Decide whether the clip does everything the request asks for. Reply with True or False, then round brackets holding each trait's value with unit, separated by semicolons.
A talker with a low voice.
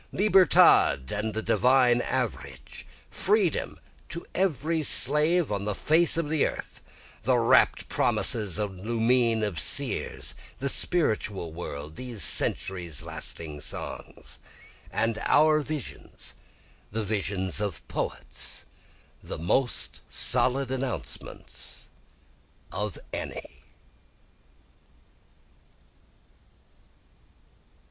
True (115 Hz)